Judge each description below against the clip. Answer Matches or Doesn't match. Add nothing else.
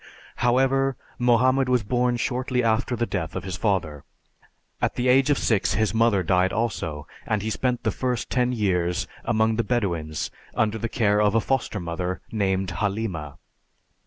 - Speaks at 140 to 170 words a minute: Matches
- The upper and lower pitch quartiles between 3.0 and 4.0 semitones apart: Doesn't match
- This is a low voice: Matches